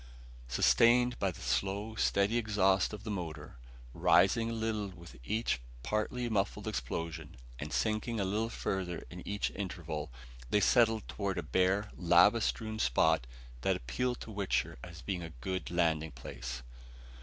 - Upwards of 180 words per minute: No, average, 150 wpm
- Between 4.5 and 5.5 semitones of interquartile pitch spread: Yes, average, 5.2 semitones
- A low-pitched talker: Yes, very low, 95 Hz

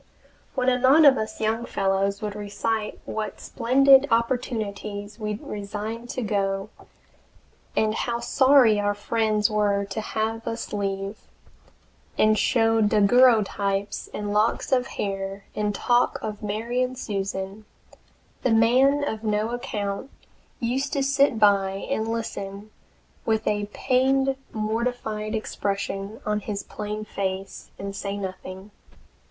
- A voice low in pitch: No, high, 215 Hz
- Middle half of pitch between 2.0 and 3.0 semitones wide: Yes, average, 2.7 semitones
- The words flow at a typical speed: No, slow, 125 wpm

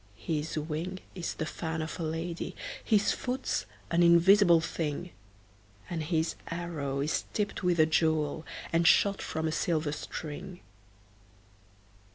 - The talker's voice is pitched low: No, medium, 165 Hz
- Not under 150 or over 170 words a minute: No, slow, 135 wpm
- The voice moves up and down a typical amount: No, narrow, 1.9 semitones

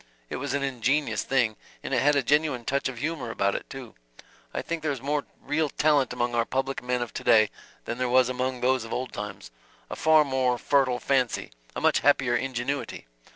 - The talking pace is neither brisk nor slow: No, fast, 210 wpm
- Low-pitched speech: Yes, low, 130 Hz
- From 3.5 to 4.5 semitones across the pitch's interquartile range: No, average, 2.7 semitones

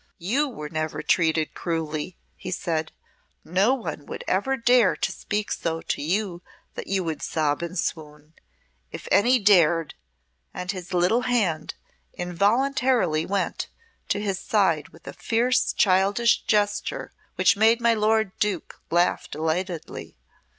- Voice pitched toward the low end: No, medium, 185 Hz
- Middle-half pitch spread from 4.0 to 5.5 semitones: Yes, average, 5.0 semitones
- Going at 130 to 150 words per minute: Yes, slow, 135 wpm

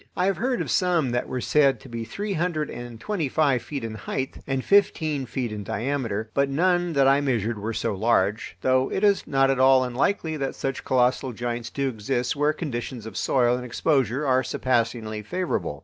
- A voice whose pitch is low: Yes, low, 130 Hz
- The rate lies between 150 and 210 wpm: Yes, average, 200 wpm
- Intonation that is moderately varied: Yes, average, 4.1 semitones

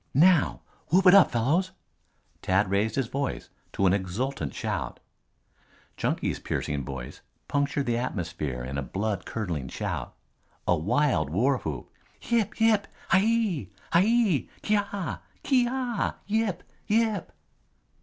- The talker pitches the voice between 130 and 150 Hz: Yes, medium, 140 Hz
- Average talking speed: No, slow, 115 wpm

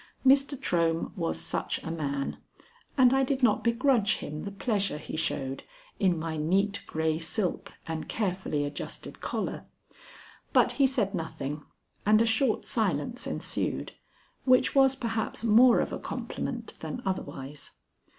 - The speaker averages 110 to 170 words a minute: Yes, average, 140 wpm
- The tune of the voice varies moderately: No, wide, 7.2 semitones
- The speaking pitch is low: No, high, 195 Hz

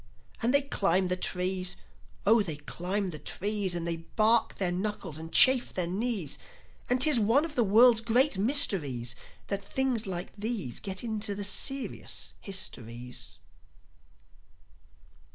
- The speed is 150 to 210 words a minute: No, average, 140 wpm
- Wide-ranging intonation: No, average, 4.7 semitones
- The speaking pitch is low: No, high, 200 Hz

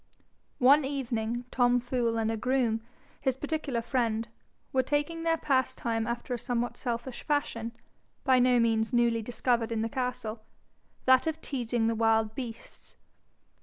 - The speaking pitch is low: No, high, 240 Hz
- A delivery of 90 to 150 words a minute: Yes, average, 145 wpm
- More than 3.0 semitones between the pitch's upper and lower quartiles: No, narrow, 2.4 semitones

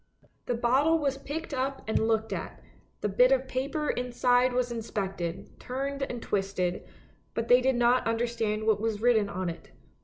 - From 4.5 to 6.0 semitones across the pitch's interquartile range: No, average, 3.3 semitones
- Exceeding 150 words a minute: Yes, average, 165 wpm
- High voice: Yes, high, 240 Hz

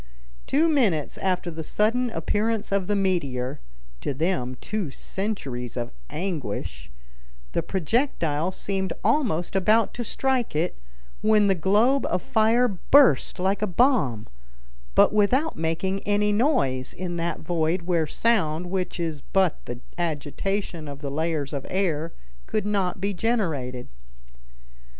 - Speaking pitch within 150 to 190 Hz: Yes, medium, 185 Hz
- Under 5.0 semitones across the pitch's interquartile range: No, average, 5.3 semitones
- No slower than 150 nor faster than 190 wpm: No, slow, 135 wpm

